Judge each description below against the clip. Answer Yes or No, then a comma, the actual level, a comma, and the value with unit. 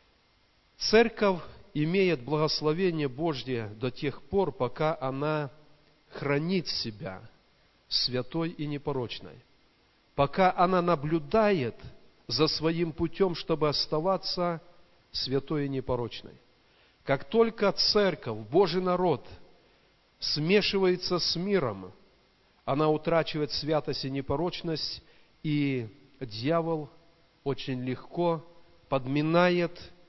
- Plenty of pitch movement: No, average, 4.2 semitones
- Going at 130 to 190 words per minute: No, slow, 85 wpm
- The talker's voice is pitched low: No, medium, 155 Hz